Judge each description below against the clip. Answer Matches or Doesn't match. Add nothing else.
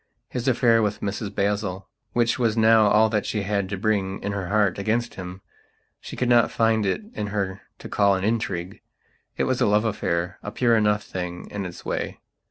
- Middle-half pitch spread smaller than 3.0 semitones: Matches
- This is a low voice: Matches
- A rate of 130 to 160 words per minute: Doesn't match